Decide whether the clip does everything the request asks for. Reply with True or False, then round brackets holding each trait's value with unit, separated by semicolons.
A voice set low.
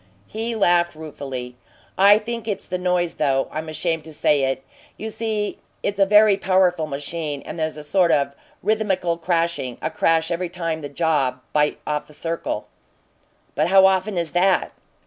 False (170 Hz)